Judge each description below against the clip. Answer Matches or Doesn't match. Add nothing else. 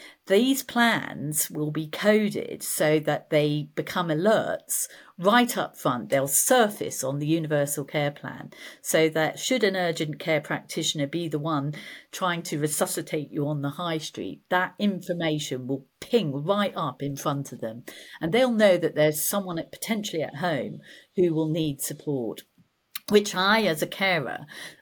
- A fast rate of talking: Doesn't match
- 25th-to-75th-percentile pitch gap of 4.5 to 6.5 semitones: Matches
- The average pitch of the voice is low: Doesn't match